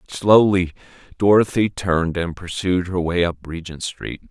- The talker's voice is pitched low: Yes, very low, 90 Hz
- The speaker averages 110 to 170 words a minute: Yes, average, 140 wpm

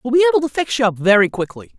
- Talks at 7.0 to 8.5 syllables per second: Yes, 7.6 syllables/s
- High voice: Yes, high, 225 Hz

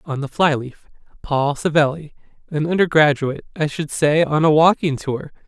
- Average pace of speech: Yes, average, 155 wpm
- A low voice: No, medium, 150 Hz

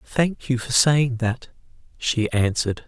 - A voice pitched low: Yes, low, 125 Hz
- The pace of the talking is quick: No, average, 145 wpm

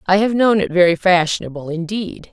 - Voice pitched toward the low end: No, medium, 185 Hz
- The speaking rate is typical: Yes, average, 180 wpm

